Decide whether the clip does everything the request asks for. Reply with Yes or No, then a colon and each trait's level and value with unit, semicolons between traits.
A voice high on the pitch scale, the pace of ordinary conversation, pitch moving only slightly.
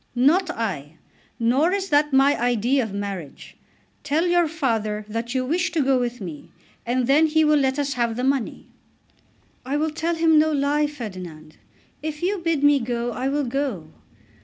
No: very high, 270 Hz; average, 180 wpm; average, 4.8 semitones